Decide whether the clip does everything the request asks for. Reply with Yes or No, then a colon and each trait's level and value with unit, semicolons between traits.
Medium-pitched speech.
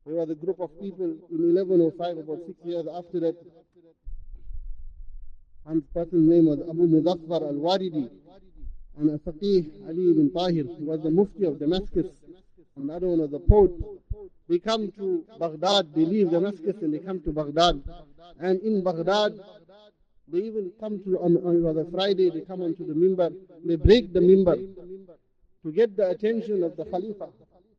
Yes: medium, 175 Hz